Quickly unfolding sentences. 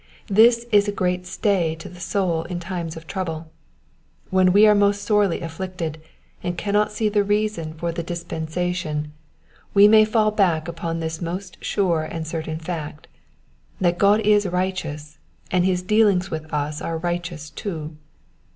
No: average, 160 wpm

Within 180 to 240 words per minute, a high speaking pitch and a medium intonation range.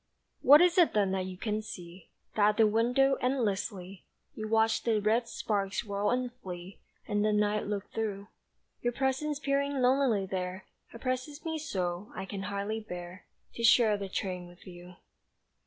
No: average, 170 wpm; high, 210 Hz; average, 4.5 semitones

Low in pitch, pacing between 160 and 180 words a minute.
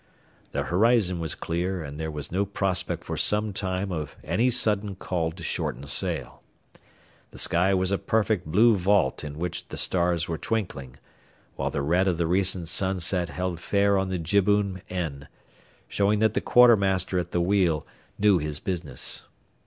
Yes: very low, 90 Hz; average, 170 wpm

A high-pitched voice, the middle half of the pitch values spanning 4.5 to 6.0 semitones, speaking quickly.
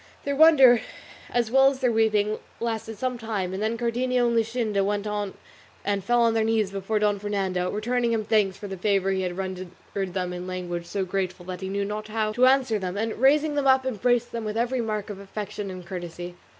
No: high, 215 Hz; average, 3.6 semitones; fast, 215 wpm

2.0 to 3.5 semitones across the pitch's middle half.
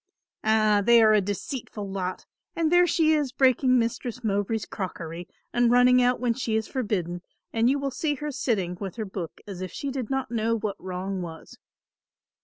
No: average, 4.6 semitones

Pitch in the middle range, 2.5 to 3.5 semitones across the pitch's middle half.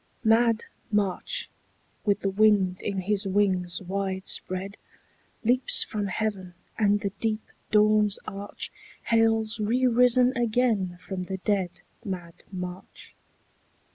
No: high, 205 Hz; average, 2.8 semitones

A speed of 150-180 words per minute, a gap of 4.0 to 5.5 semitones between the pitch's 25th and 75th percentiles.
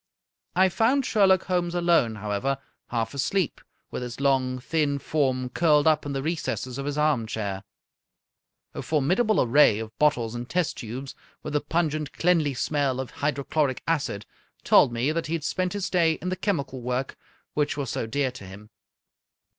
Yes: average, 170 wpm; average, 4.8 semitones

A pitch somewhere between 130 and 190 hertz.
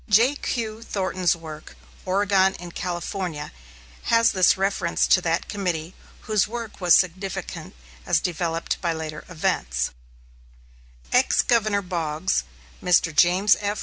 Yes: medium, 185 Hz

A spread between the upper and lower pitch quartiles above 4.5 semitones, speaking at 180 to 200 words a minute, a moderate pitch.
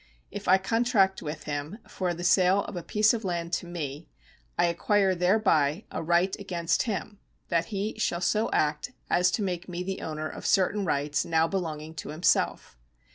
No: average, 3.4 semitones; average, 185 wpm; medium, 180 Hz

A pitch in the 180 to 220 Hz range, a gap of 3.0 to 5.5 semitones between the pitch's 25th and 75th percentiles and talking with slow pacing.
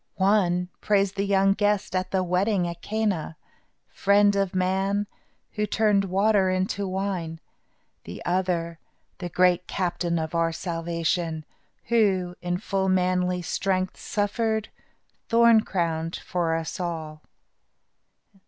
No: medium, 185 Hz; narrow, 2.6 semitones; slow, 120 wpm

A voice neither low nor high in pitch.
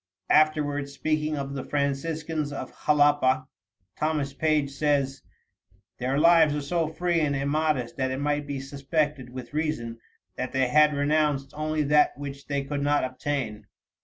Yes: medium, 145 Hz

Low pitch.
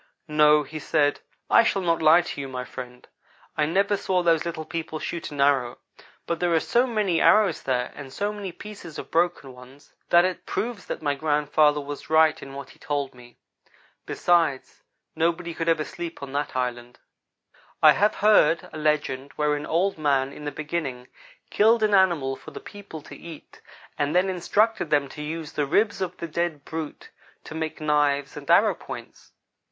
No: medium, 155 Hz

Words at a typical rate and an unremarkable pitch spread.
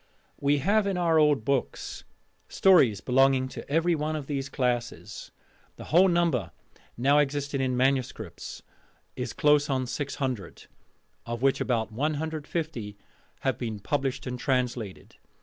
No: slow, 130 wpm; average, 3.3 semitones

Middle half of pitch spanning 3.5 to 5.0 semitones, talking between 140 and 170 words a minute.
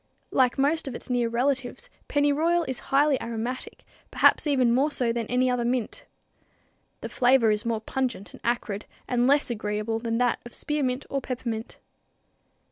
No: average, 2.8 semitones; average, 160 wpm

